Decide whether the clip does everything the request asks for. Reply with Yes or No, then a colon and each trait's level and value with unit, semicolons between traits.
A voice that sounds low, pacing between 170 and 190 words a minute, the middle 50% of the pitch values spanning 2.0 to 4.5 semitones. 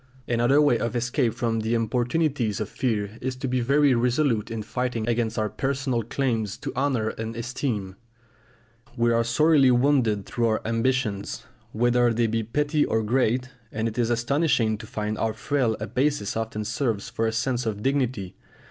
Yes: low, 120 Hz; average, 175 wpm; average, 2.8 semitones